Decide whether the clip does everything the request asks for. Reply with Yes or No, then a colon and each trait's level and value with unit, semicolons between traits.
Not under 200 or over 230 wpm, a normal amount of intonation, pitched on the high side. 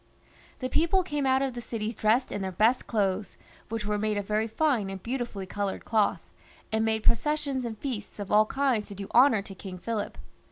Yes: fast, 205 wpm; average, 3.8 semitones; high, 220 Hz